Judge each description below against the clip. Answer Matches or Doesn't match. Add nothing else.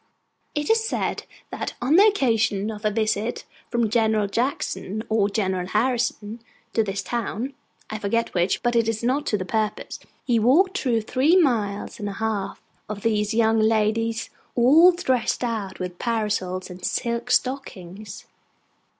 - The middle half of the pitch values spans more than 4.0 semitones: Doesn't match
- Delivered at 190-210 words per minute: Doesn't match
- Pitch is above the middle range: Matches